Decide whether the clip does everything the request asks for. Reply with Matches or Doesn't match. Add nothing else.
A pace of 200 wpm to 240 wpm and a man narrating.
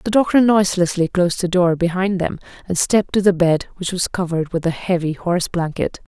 Doesn't match